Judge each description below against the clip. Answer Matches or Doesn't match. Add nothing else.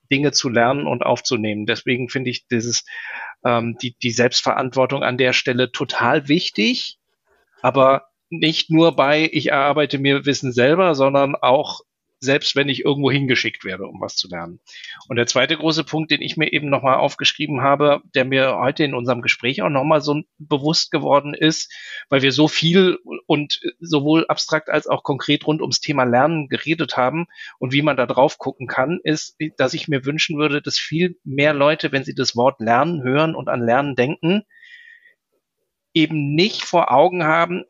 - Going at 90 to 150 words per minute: Doesn't match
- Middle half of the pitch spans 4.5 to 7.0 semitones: Doesn't match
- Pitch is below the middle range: Doesn't match